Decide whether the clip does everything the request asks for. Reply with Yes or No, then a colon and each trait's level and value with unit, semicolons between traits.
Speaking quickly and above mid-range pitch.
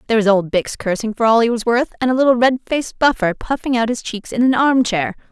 Yes: fast, 260 wpm; high, 230 Hz